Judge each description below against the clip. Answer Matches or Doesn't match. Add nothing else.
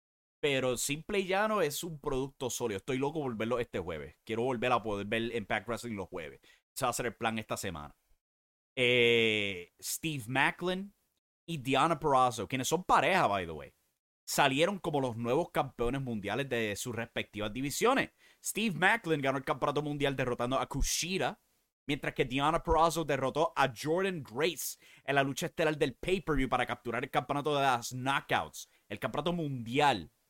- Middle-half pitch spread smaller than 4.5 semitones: Doesn't match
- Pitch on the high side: Doesn't match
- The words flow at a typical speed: Matches